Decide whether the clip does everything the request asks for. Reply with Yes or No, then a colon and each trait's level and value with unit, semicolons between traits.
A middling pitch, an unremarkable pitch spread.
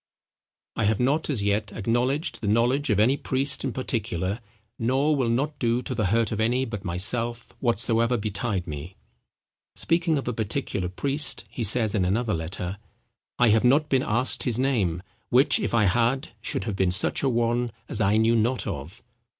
No: low, 115 Hz; average, 4.0 semitones